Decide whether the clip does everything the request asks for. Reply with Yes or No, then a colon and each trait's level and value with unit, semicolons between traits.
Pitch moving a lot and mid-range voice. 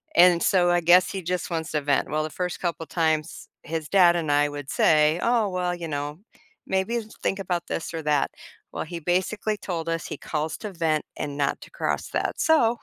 No: average, 2.9 semitones; medium, 170 Hz